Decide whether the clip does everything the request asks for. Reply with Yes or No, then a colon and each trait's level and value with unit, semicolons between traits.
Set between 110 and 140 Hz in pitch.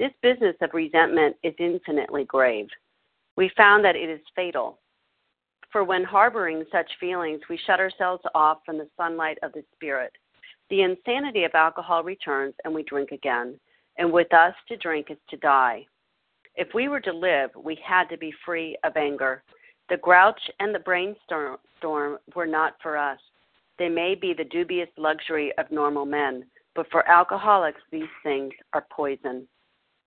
No: medium, 165 Hz